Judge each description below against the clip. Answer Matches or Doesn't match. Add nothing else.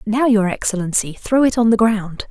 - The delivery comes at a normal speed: Doesn't match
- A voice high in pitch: Matches